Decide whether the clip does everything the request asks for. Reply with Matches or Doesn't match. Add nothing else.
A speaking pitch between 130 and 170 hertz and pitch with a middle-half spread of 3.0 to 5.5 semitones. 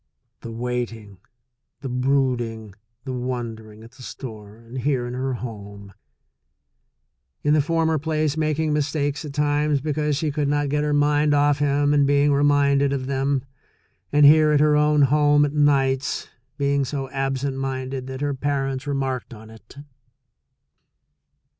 Doesn't match